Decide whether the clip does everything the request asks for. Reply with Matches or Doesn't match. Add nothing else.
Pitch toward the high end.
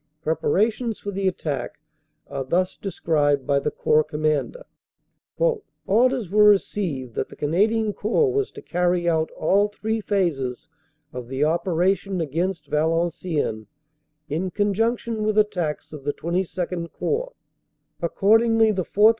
Doesn't match